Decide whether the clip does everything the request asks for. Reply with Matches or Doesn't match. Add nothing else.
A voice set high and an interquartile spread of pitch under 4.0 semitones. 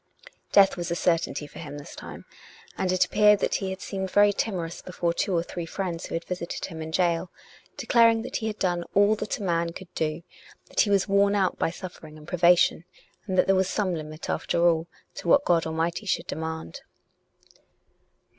Doesn't match